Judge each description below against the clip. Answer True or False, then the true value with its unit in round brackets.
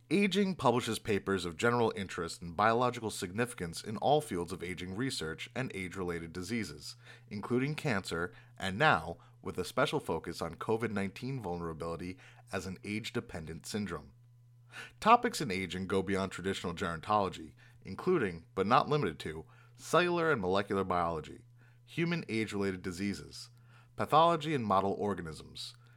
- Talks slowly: True (130 wpm)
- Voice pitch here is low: True (105 Hz)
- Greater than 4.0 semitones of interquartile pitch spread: True (4.7 semitones)